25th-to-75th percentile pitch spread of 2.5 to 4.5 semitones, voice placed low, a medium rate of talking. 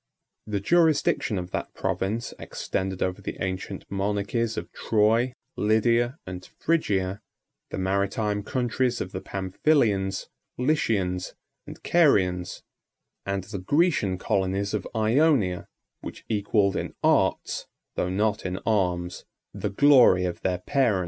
No: average, 4.0 semitones; low, 100 Hz; slow, 120 wpm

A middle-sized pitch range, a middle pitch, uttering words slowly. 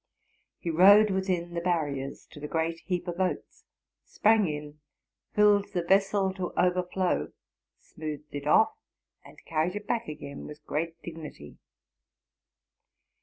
Yes: average, 3.9 semitones; medium, 175 Hz; slow, 130 wpm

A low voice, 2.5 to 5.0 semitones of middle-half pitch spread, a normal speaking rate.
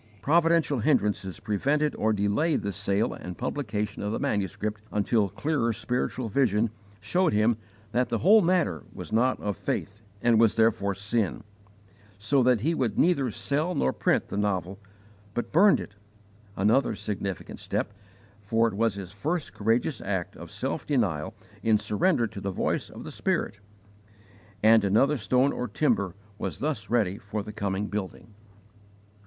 Yes: low, 110 Hz; average, 4.7 semitones; average, 155 wpm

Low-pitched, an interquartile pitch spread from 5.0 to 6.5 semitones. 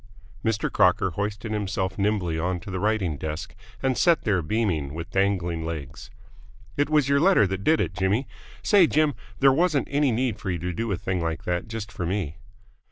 Yes: low, 100 Hz; wide, 5.5 semitones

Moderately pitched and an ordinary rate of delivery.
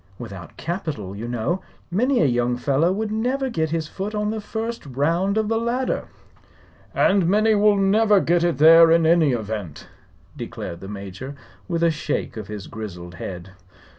Yes: medium, 165 Hz; average, 170 wpm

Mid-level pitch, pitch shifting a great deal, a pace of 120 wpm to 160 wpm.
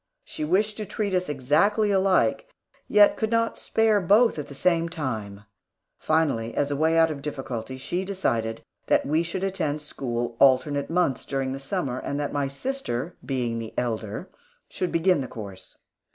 No: medium, 150 Hz; wide, 6.2 semitones; average, 175 wpm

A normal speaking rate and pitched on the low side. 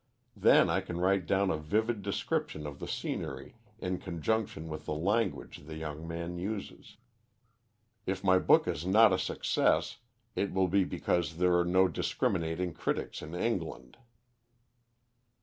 Yes: average, 150 wpm; very low, 90 Hz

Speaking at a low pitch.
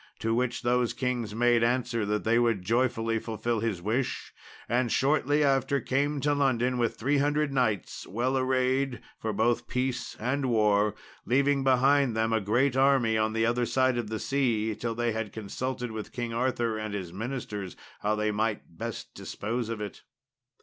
Yes: low, 120 Hz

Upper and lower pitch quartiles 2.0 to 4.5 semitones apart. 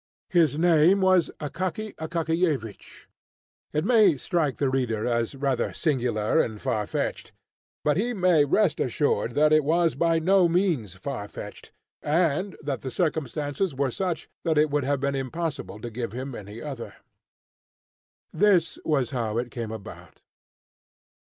No: average, 5.3 semitones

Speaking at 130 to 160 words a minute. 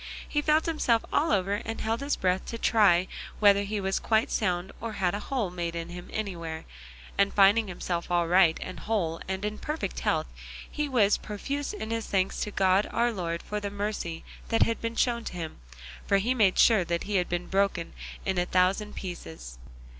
No: average, 195 wpm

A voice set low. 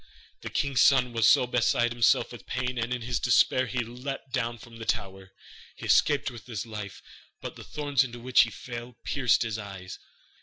Yes: low, 120 Hz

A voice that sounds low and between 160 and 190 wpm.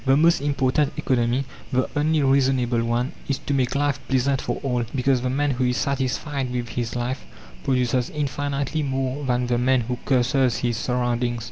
Yes: low, 130 Hz; average, 175 wpm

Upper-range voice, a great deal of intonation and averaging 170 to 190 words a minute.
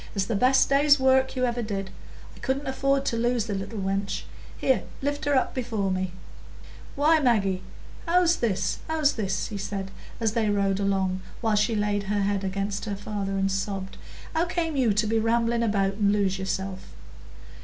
No: high, 210 Hz; average, 4.9 semitones; average, 185 wpm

